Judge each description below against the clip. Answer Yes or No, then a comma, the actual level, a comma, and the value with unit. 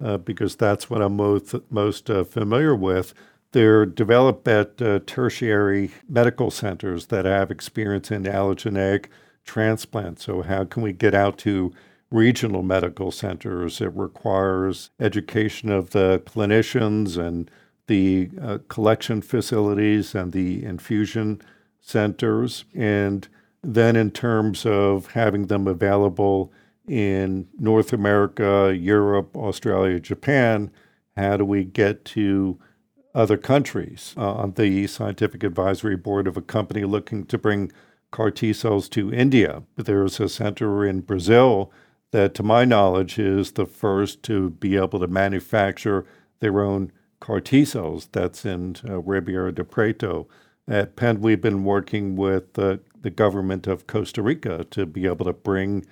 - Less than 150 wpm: Yes, average, 140 wpm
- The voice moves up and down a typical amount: No, narrow, 2.3 semitones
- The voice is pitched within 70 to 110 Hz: Yes, low, 100 Hz